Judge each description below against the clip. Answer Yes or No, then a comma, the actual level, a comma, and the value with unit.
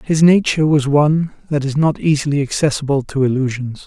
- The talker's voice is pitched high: No, medium, 145 Hz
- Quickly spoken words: No, average, 170 wpm